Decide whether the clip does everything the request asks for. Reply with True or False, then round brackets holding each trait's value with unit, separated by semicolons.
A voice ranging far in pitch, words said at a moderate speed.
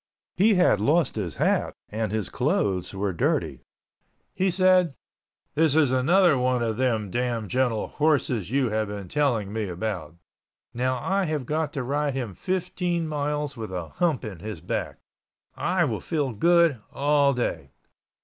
True (6.4 semitones; 160 wpm)